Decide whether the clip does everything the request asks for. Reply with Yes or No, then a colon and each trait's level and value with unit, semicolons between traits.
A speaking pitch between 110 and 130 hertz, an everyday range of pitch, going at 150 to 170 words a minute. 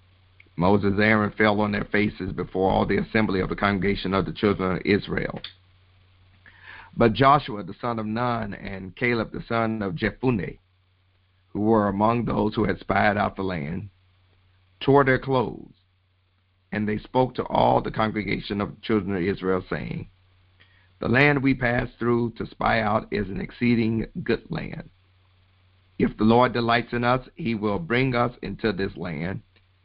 No: low, 100 Hz; average, 3.6 semitones; average, 165 wpm